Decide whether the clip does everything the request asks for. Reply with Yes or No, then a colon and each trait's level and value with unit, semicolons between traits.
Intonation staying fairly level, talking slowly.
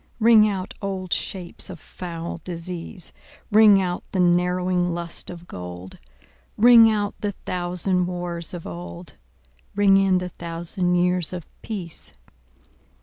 Yes: narrow, 2.2 semitones; slow, 130 wpm